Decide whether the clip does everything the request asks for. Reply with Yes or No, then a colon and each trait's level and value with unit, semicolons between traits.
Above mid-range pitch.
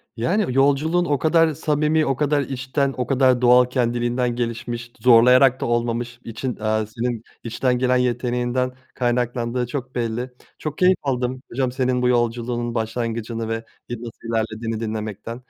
No: low, 125 Hz